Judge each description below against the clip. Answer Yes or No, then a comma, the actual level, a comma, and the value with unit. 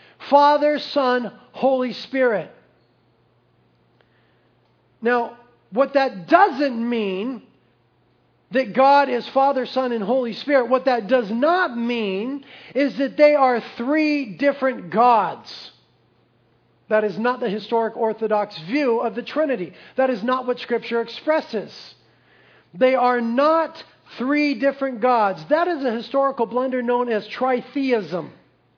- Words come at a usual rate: No, slow, 125 wpm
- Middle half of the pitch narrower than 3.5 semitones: Yes, average, 2.9 semitones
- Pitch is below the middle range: No, very high, 255 Hz